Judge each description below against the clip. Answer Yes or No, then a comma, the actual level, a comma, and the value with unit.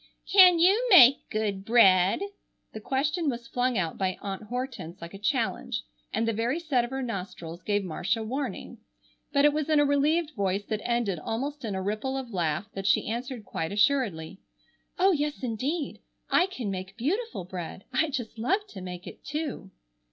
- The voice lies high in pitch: Yes, high, 235 Hz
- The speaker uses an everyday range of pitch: No, wide, 6.5 semitones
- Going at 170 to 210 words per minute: Yes, average, 180 wpm